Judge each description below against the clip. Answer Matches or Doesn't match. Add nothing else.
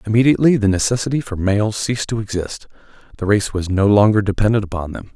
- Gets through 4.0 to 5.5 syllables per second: Doesn't match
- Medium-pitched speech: Doesn't match